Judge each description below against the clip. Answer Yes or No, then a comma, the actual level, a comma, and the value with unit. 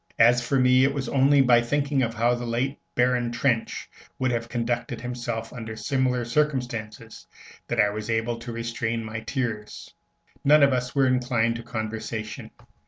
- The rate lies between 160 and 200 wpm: Yes, average, 165 wpm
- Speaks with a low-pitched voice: Yes, low, 120 Hz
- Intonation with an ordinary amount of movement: No, narrow, 2.0 semitones